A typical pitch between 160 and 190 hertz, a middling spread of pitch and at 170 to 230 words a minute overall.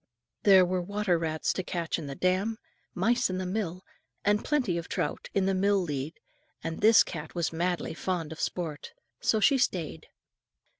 Yes: medium, 185 Hz; average, 3.7 semitones; average, 180 wpm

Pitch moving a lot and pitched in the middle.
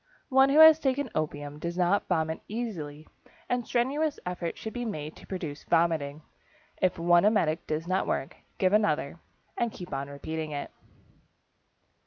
Yes: wide, 6.6 semitones; medium, 175 Hz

